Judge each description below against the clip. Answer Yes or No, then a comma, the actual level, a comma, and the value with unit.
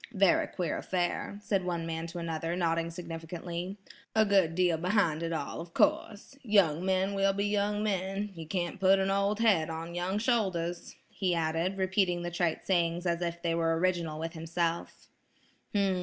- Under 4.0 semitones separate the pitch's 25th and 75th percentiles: Yes, average, 2.8 semitones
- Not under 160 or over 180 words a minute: Yes, average, 170 wpm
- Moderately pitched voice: Yes, medium, 175 Hz